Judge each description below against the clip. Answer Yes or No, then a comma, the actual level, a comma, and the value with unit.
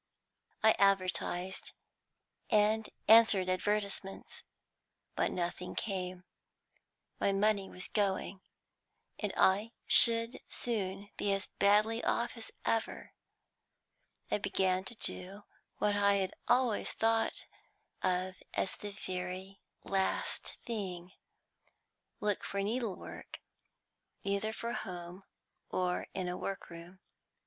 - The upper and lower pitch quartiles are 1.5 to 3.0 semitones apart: Yes, narrow, 2.6 semitones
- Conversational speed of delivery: No, slow, 105 wpm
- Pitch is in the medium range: No, high, 195 Hz